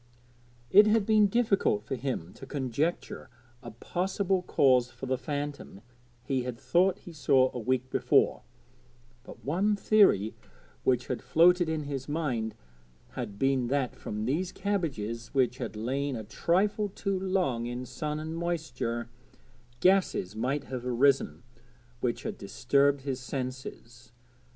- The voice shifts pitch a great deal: Yes, wide, 5.9 semitones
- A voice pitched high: No, low, 135 Hz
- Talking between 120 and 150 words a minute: Yes, average, 140 wpm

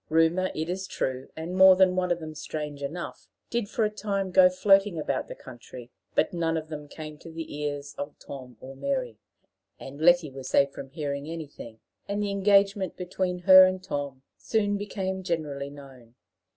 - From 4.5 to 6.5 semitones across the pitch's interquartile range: Yes, average, 4.9 semitones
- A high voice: No, medium, 165 Hz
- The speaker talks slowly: No, average, 190 wpm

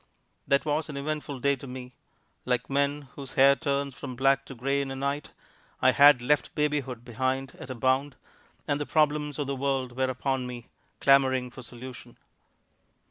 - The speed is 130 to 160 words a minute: No, average, 180 wpm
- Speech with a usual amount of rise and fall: No, narrow, 1.7 semitones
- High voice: No, low, 135 Hz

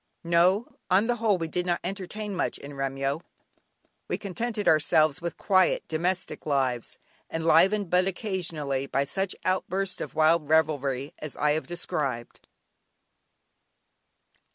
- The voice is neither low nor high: Yes, medium, 170 Hz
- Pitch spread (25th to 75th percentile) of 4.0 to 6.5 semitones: Yes, average, 4.3 semitones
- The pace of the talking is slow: Yes, slow, 130 wpm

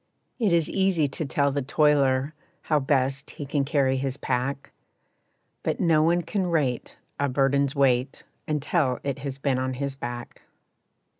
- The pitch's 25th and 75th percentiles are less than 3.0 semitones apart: Yes, narrow, 2.4 semitones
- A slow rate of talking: No, average, 155 wpm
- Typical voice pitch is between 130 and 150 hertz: Yes, medium, 140 Hz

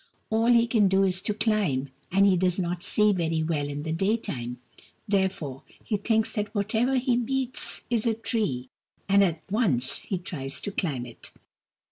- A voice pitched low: No, high, 195 Hz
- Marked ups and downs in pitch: Yes, wide, 5.8 semitones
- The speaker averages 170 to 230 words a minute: Yes, average, 175 wpm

